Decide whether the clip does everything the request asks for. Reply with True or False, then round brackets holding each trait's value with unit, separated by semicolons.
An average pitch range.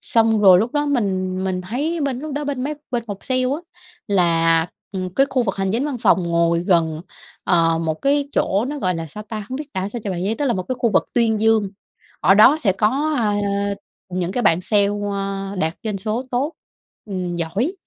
False (5.7 semitones)